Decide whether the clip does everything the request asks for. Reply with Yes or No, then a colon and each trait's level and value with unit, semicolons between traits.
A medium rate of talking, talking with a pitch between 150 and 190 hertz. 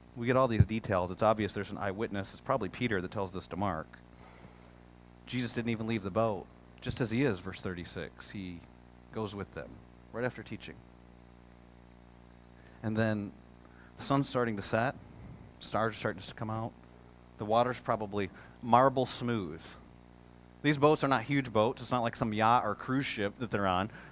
No: average, 180 wpm; low, 100 Hz